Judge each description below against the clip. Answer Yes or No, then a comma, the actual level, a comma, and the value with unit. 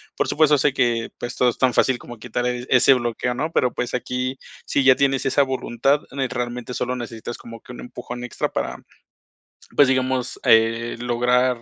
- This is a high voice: No, low, 125 Hz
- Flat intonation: Yes, narrow, 1.5 semitones